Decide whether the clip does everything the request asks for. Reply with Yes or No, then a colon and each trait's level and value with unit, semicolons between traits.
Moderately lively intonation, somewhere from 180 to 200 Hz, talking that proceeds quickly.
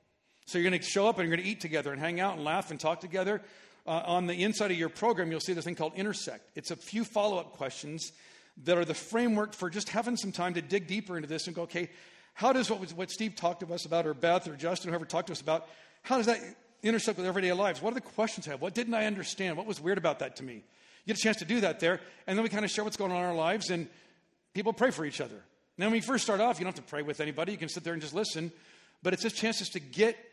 Yes: average, 4.0 semitones; medium, 185 Hz; fast, 300 wpm